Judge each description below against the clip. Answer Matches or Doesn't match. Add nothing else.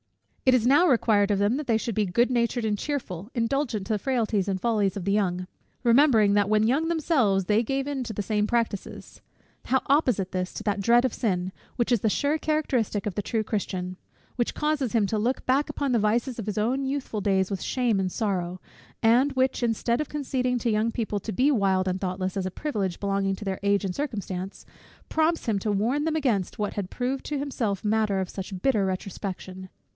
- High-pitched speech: Matches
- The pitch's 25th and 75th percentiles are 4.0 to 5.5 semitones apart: Matches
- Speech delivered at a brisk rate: Matches